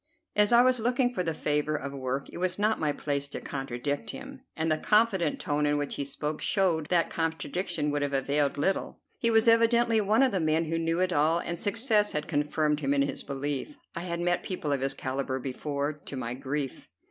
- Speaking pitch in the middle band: Yes, medium, 155 Hz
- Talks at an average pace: No, fast, 220 wpm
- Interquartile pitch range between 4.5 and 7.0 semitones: Yes, average, 5.2 semitones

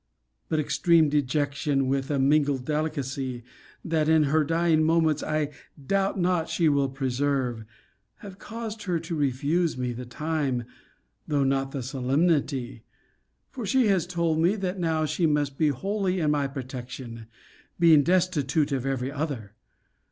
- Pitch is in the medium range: Yes, medium, 150 Hz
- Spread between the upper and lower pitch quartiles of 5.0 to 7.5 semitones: No, average, 3.7 semitones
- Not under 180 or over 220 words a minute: No, average, 145 wpm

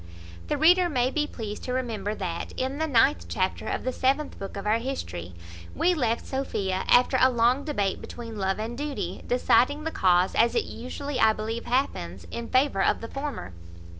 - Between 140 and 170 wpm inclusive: No, average, 190 wpm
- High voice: Yes, high, 240 Hz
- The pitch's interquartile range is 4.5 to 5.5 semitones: Yes, average, 5.1 semitones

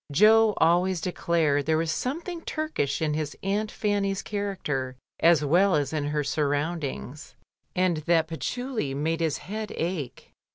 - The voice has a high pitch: No, medium, 165 Hz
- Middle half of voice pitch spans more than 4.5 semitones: Yes, average, 5.2 semitones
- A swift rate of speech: No, average, 150 wpm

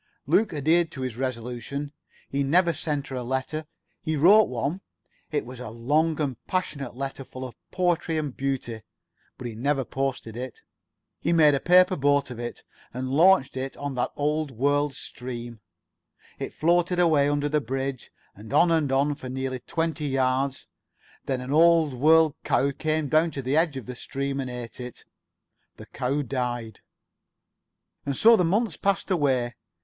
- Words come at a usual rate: Yes, average, 170 wpm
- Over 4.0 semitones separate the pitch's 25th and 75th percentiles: No, average, 3.6 semitones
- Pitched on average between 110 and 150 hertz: Yes, medium, 140 Hz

